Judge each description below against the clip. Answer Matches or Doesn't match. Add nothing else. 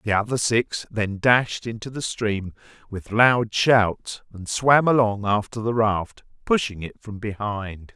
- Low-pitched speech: Matches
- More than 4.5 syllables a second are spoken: Doesn't match